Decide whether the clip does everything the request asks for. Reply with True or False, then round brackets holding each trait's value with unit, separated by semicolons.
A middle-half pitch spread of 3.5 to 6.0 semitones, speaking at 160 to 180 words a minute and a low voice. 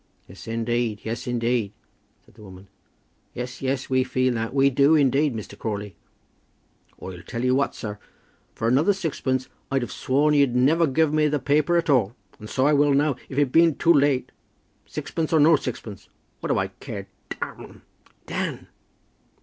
True (3.9 semitones; 175 wpm; 130 Hz)